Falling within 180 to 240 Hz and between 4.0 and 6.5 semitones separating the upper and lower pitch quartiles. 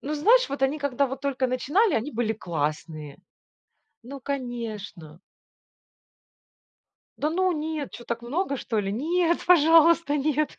No: very high, 275 Hz; average, 5.1 semitones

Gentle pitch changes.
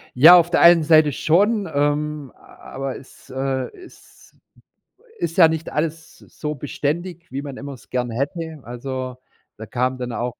No: average, 3.9 semitones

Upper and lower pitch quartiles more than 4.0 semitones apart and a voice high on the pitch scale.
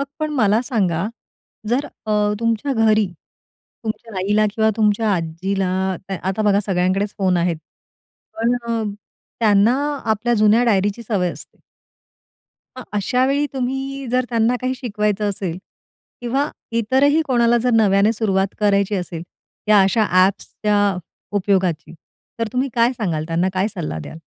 No: average, 3.5 semitones; high, 210 Hz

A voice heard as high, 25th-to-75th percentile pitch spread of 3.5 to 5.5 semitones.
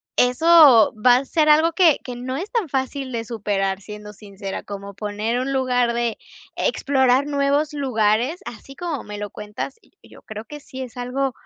Yes: very high, 250 Hz; average, 4.7 semitones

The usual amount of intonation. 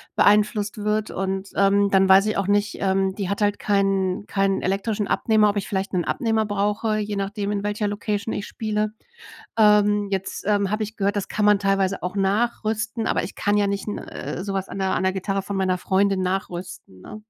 No: narrow, 1.5 semitones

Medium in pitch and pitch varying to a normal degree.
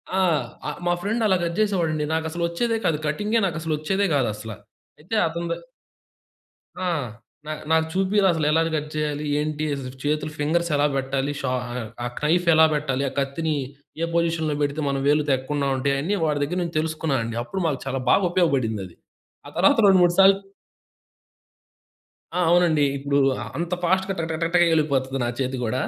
Yes: medium, 155 Hz; average, 3.5 semitones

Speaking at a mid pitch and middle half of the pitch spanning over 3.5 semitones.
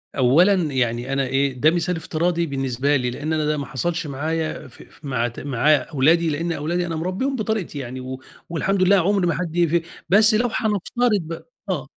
Yes: medium, 160 Hz; average, 4.6 semitones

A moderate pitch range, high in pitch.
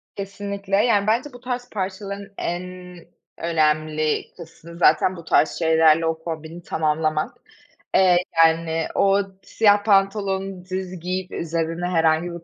No: average, 3.4 semitones; medium, 175 Hz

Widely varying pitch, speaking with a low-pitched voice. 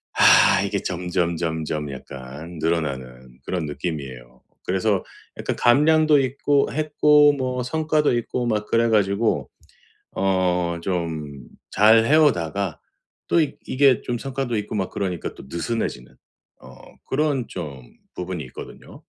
Yes: wide, 8.1 semitones; very low, 95 Hz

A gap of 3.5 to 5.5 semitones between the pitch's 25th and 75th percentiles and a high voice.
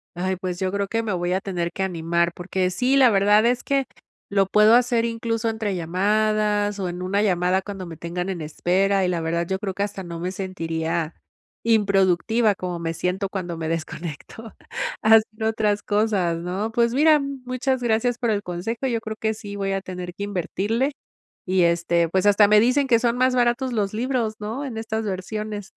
Yes: average, 3.8 semitones; high, 200 Hz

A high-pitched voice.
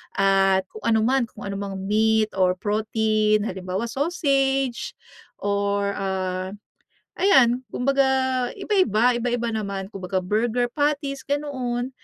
Yes: high, 220 Hz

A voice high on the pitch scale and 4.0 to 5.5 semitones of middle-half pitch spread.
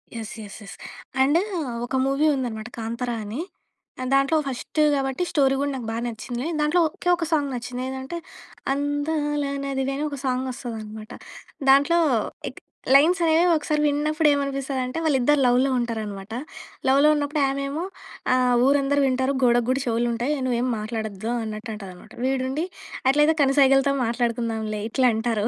No: very high, 265 Hz; average, 3.5 semitones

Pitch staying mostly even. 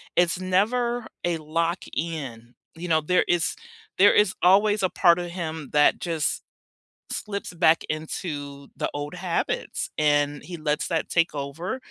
No: average, 3.4 semitones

